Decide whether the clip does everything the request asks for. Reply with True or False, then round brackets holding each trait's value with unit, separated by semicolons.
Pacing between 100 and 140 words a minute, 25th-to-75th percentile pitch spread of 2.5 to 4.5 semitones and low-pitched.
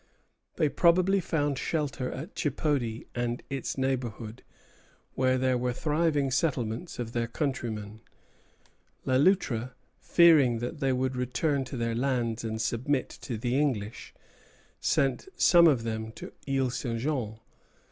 True (135 wpm; 3.8 semitones; 130 Hz)